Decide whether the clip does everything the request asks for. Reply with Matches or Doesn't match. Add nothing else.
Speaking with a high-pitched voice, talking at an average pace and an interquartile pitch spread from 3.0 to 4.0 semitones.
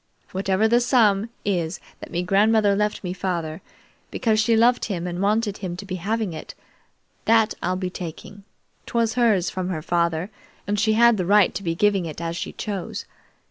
Matches